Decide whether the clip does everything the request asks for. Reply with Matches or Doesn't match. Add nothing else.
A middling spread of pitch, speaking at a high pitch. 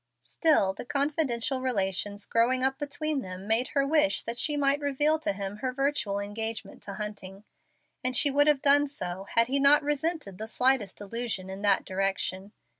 Doesn't match